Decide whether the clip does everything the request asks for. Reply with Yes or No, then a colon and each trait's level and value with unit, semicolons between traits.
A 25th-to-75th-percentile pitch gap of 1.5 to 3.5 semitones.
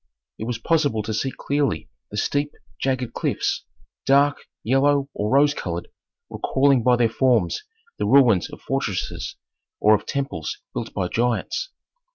No: average, 4.4 semitones